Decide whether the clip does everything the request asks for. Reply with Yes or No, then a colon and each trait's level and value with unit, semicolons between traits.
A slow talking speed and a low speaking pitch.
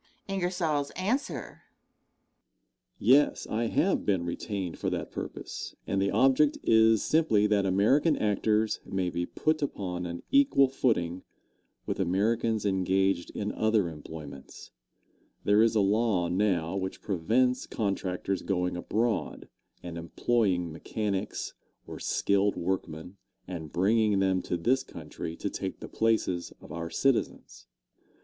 Yes: slow, 125 wpm; low, 100 Hz